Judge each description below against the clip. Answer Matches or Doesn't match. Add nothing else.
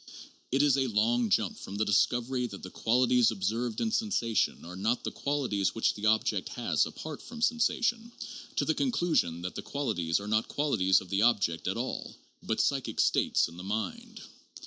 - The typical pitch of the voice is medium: Doesn't match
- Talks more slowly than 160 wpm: Doesn't match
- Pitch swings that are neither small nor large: Doesn't match